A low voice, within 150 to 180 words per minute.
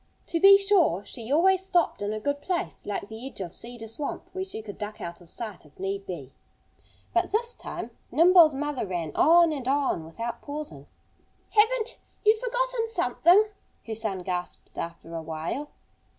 No: very high, 270 Hz; average, 175 wpm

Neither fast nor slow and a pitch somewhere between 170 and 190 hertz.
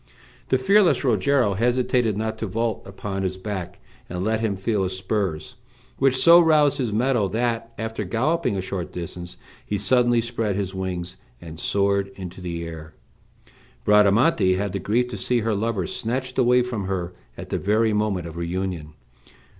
No: average, 170 wpm; low, 105 Hz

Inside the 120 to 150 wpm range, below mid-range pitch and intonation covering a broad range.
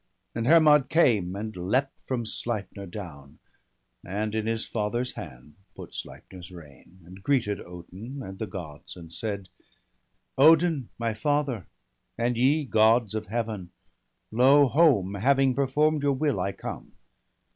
Yes: average, 145 wpm; low, 110 Hz; wide, 6.0 semitones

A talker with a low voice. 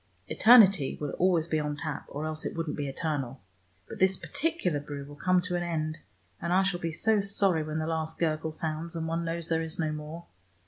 No: medium, 160 Hz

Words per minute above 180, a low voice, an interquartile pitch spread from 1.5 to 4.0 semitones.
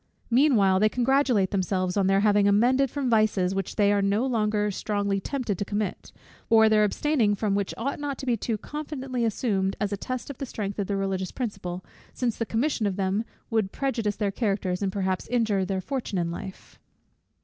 No: average, 195 wpm; high, 210 Hz; average, 3.7 semitones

